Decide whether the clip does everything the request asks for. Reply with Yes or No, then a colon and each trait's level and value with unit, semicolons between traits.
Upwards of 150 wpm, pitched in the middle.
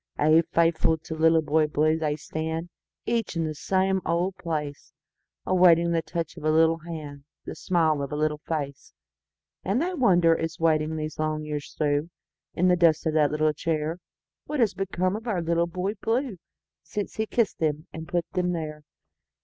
Yes: average, 160 wpm; medium, 165 Hz